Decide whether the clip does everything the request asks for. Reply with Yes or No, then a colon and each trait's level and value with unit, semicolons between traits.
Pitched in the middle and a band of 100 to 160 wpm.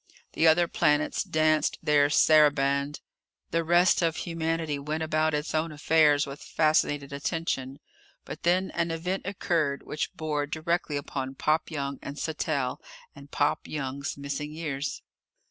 Yes: medium, 155 Hz; average, 140 wpm